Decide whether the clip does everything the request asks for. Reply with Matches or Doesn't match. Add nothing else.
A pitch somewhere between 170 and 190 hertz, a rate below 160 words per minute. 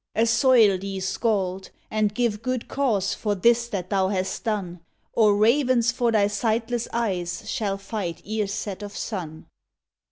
Doesn't match